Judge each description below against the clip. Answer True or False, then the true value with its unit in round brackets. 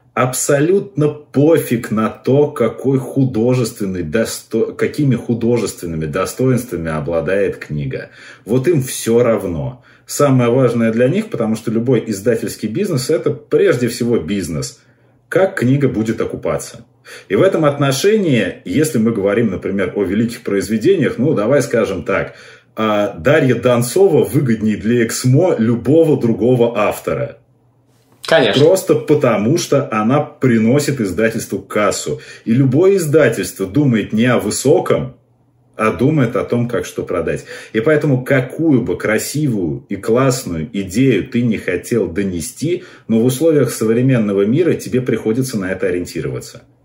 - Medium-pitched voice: False (120 Hz)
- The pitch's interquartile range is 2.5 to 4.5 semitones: True (3.3 semitones)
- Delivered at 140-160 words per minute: False (125 wpm)